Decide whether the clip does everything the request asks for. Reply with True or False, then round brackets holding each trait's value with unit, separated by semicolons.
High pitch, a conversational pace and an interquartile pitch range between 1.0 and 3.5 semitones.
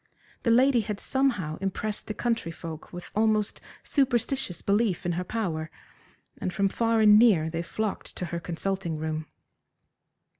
False (200 Hz; 150 wpm; 5.1 semitones)